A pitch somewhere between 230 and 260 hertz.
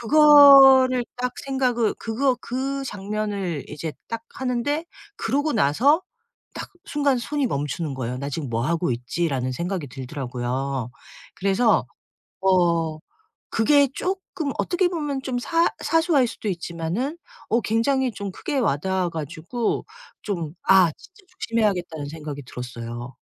No: high, 210 Hz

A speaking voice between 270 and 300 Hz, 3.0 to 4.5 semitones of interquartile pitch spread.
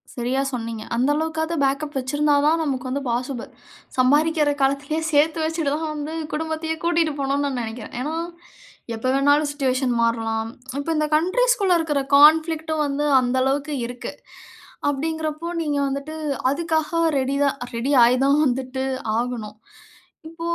Yes: very high, 285 Hz; average, 3.4 semitones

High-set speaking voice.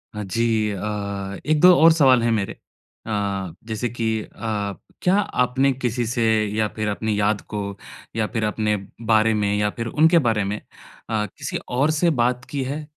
No: low, 115 Hz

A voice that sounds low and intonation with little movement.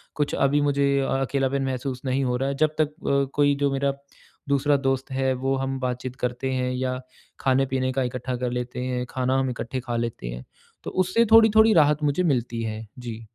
Yes: low, 130 Hz; narrow, 2.0 semitones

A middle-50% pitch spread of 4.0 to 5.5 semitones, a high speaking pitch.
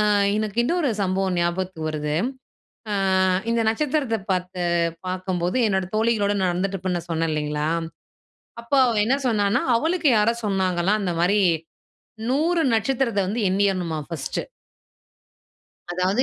Yes: average, 4.3 semitones; high, 195 Hz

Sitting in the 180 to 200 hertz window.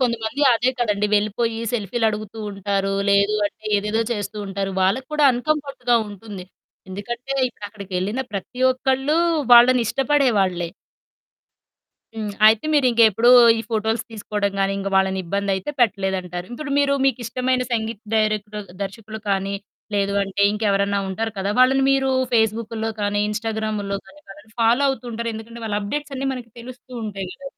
No: high, 220 Hz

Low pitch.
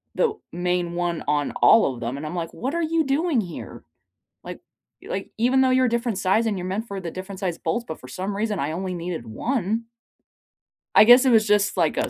No: high, 195 Hz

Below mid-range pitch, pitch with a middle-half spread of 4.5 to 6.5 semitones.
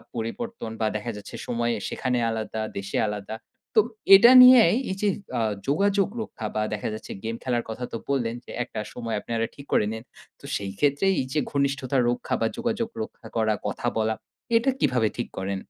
Yes: low, 120 Hz; average, 5.2 semitones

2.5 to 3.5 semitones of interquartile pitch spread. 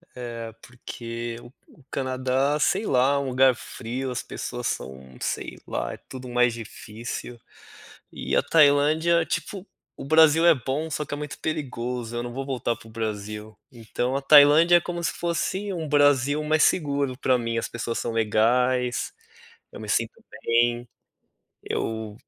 No: average, 4.0 semitones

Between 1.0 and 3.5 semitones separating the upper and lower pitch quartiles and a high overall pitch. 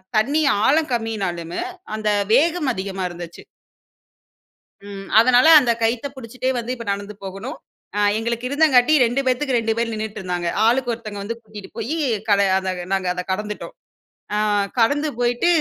No: average, 3.9 semitones; high, 225 Hz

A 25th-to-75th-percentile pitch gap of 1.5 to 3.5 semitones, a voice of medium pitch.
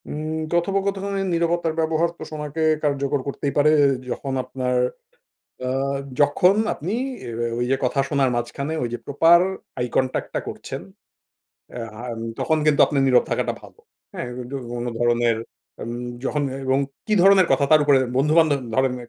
No: average, 4.3 semitones; medium, 145 Hz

